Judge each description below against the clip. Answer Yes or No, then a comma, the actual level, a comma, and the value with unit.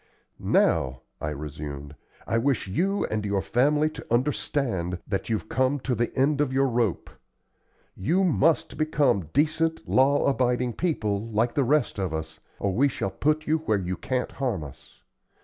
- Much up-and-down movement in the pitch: Yes, wide, 6.9 semitones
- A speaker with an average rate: Yes, average, 165 wpm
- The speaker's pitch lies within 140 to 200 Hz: No, low, 125 Hz